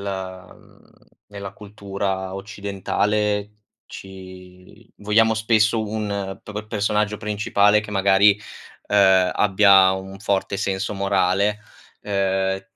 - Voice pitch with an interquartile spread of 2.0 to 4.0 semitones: No, narrow, 1.6 semitones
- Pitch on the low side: Yes, low, 100 Hz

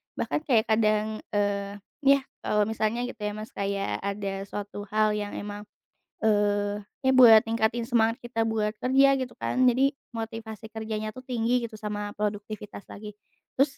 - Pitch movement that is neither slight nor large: No, narrow, 2.2 semitones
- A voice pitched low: No, high, 215 Hz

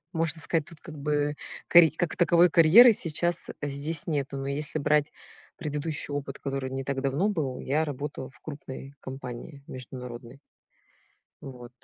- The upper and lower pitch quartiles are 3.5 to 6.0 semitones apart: No, average, 2.9 semitones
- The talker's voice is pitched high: No, medium, 145 Hz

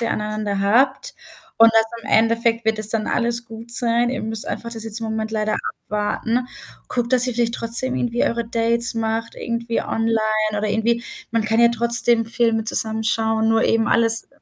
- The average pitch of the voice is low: No, high, 230 Hz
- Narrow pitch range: Yes, narrow, 1.1 semitones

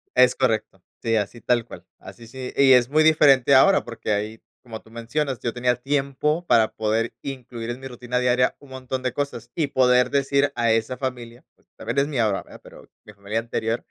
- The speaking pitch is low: Yes, low, 125 Hz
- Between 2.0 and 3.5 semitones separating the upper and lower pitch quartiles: Yes, average, 2.8 semitones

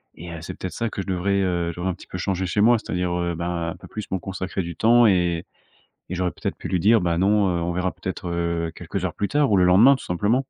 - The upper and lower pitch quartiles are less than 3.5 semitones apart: Yes, narrow, 2.5 semitones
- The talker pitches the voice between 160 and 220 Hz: No, very low, 90 Hz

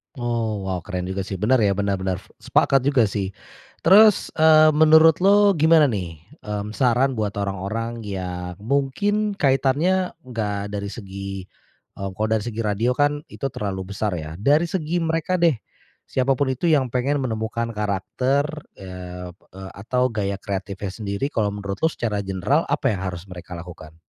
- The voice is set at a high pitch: No, low, 110 Hz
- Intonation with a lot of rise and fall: Yes, wide, 6.2 semitones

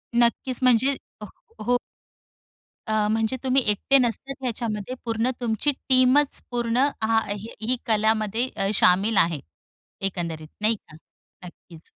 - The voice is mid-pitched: No, high, 225 Hz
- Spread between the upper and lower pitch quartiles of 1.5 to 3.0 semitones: No, average, 3.4 semitones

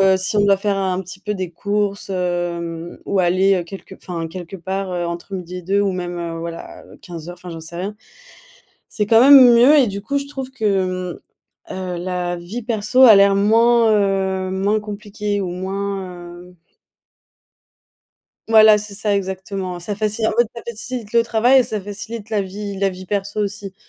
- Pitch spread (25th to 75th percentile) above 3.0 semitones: No, narrow, 2.6 semitones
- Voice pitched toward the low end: No, high, 195 Hz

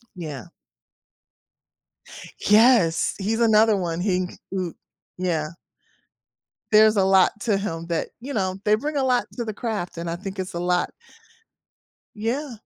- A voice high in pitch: Yes, high, 195 Hz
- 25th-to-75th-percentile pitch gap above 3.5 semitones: Yes, average, 4.0 semitones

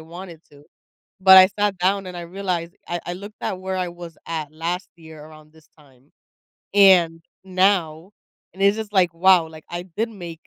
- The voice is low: No, medium, 175 Hz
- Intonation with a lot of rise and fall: No, average, 2.9 semitones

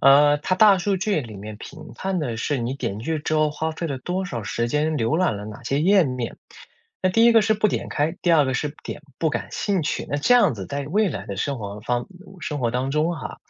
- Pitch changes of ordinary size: No, wide, 6.6 semitones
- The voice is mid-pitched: Yes, medium, 150 Hz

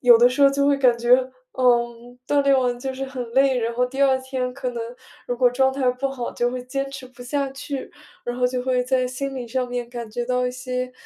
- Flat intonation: Yes, narrow, 1.5 semitones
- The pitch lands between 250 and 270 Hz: Yes, very high, 255 Hz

